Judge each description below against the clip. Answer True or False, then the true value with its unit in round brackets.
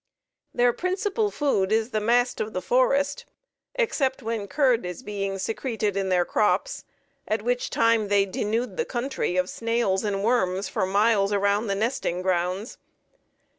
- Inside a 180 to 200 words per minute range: False (155 wpm)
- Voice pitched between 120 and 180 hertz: False (220 Hz)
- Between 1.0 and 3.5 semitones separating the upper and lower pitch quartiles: False (4.0 semitones)